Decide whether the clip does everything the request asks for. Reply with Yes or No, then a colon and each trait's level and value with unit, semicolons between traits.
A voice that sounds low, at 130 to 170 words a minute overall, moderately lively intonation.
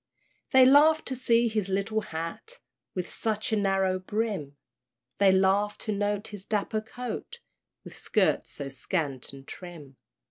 No: high, 200 Hz; average, 145 wpm; average, 3.5 semitones